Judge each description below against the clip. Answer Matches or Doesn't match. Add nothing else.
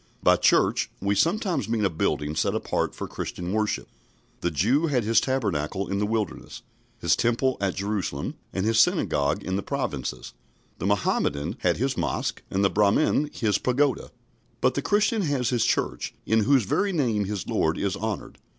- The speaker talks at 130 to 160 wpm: Doesn't match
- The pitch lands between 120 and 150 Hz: Doesn't match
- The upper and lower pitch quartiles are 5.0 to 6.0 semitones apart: Matches